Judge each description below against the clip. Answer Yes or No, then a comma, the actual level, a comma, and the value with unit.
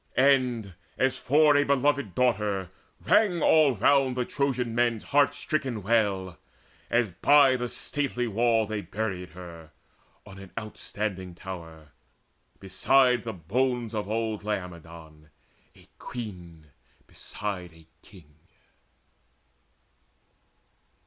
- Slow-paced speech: Yes, slow, 110 wpm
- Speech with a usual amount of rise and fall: No, wide, 5.7 semitones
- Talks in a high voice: No, low, 110 Hz